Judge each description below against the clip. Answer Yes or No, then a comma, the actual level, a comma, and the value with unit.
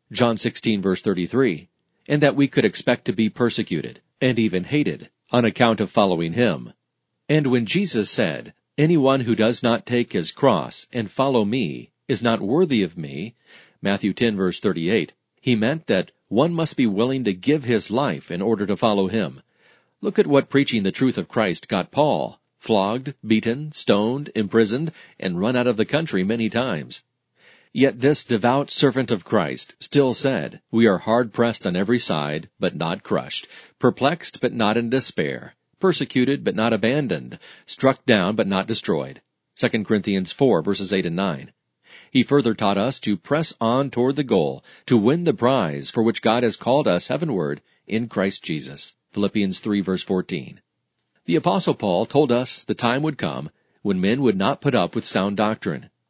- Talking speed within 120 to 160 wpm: No, average, 180 wpm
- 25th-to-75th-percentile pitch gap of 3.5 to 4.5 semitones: Yes, average, 4.1 semitones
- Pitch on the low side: Yes, low, 120 Hz